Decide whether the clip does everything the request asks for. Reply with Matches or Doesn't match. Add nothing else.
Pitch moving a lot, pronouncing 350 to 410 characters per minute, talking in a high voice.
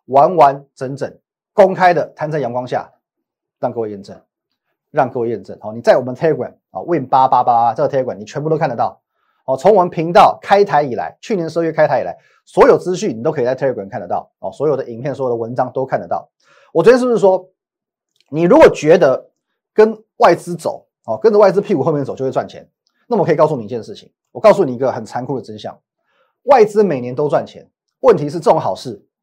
Doesn't match